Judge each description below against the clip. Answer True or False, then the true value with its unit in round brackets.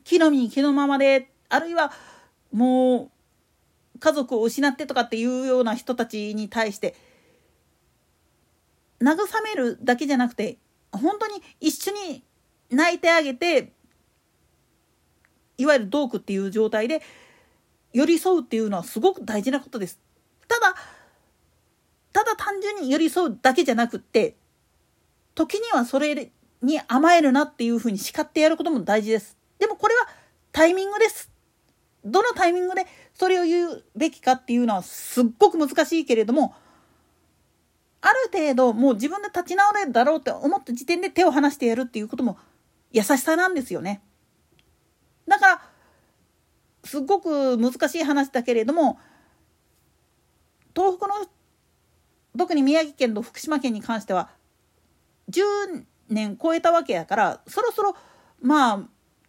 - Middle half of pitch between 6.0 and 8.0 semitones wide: True (6.3 semitones)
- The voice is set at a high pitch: True (285 Hz)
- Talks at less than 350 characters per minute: True (290 characters per minute)